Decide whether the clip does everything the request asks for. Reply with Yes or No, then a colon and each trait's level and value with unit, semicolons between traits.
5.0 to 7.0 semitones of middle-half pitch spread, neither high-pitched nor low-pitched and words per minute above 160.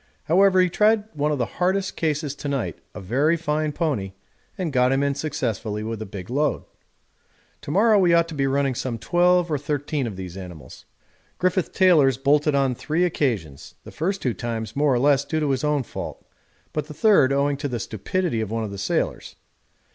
Yes: wide, 5.4 semitones; medium, 145 Hz; average, 200 wpm